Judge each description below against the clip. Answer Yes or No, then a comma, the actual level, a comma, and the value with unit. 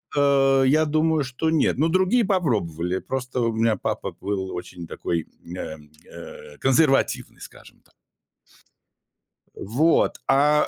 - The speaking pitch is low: Yes, low, 130 Hz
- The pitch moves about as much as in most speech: No, wide, 8.6 semitones